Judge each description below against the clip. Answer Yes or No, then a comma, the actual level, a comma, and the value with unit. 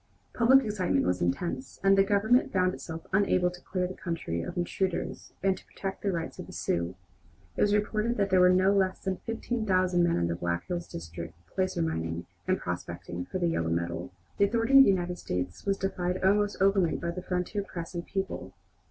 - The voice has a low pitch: No, medium, 185 Hz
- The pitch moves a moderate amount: Yes, average, 3.3 semitones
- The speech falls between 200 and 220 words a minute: Yes, fast, 205 wpm